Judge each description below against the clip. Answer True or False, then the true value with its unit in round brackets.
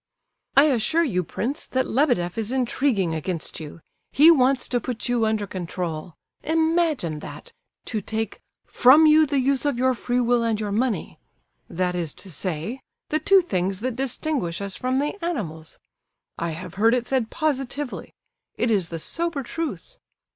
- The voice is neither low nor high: False (240 Hz)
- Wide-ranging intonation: True (7.2 semitones)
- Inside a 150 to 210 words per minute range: True (160 wpm)